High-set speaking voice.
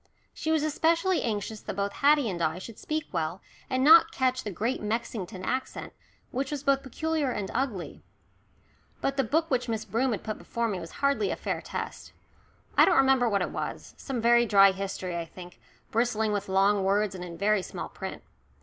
Yes: high, 225 Hz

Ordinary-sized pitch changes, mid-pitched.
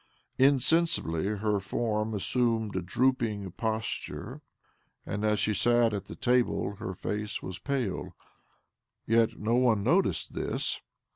No: average, 3.3 semitones; low, 110 Hz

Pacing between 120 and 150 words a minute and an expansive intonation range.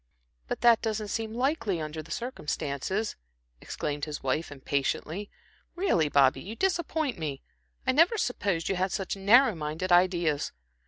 Yes: average, 145 wpm; wide, 7.1 semitones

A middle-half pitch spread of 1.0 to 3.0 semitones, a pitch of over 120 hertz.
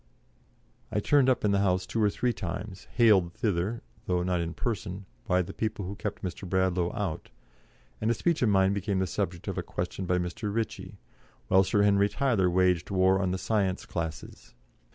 No: narrow, 2.5 semitones; very low, 95 Hz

